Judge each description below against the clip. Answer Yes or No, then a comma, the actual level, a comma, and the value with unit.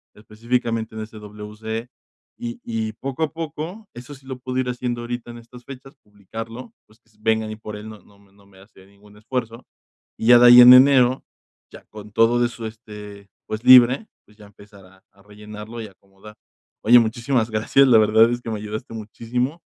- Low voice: Yes, low, 115 Hz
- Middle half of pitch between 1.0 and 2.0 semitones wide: No, average, 2.7 semitones